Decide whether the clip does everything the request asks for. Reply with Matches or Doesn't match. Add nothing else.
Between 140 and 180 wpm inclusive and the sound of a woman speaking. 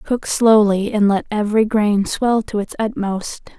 Matches